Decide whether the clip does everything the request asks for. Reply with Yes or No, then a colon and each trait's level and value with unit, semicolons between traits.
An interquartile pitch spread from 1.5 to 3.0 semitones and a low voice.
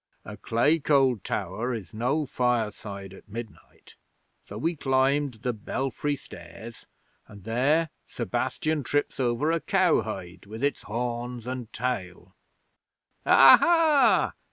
No: average, 4.7 semitones; low, 125 Hz